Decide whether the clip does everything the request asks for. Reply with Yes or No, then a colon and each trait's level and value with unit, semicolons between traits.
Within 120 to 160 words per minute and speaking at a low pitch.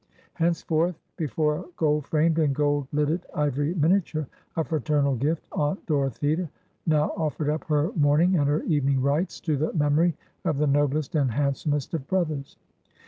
No: average, 155 wpm; medium, 150 Hz